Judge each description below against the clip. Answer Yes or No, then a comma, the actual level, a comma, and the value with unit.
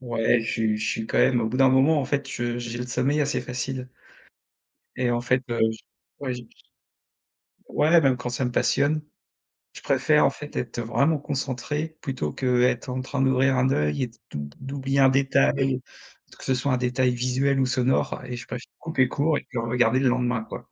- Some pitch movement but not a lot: No, narrow, 2.0 semitones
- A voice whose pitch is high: No, low, 130 Hz